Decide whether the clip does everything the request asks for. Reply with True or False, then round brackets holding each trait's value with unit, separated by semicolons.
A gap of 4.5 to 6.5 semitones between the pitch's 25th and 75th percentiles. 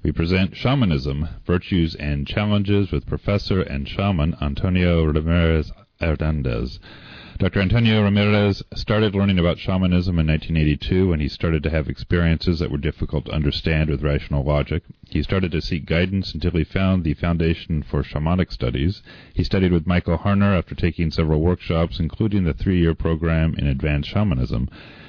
False (3.7 semitones)